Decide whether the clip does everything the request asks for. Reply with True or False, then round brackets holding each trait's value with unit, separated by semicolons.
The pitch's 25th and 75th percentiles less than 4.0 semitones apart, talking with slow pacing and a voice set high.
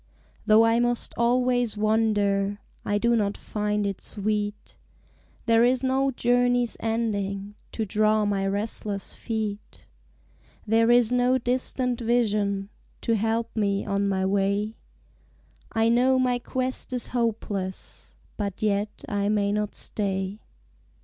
True (2.8 semitones; 125 wpm; 215 Hz)